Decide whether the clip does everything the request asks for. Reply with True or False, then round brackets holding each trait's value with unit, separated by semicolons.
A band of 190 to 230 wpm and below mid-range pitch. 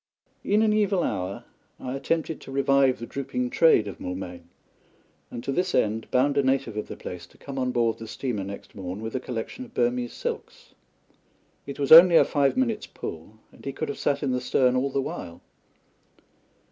True (195 wpm; 130 Hz)